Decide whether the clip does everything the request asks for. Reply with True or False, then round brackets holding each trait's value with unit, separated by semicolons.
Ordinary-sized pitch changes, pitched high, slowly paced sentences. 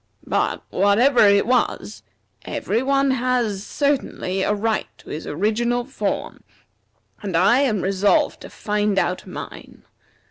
True (4.0 semitones; 215 Hz; 130 wpm)